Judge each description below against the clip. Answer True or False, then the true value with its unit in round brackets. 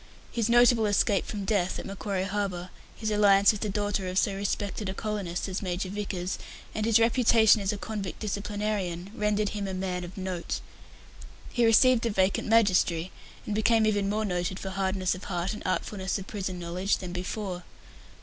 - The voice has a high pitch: True (200 Hz)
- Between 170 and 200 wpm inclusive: True (180 wpm)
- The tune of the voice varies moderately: False (2.3 semitones)